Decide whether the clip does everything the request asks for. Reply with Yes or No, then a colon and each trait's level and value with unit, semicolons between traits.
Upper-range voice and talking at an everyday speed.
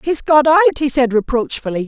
Yes: very high, 265 Hz; average, 190 wpm